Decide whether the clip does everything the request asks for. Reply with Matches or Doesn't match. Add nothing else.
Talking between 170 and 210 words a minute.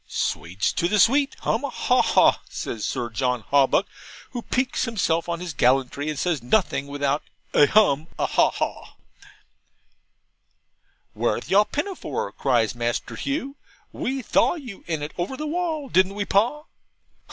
Doesn't match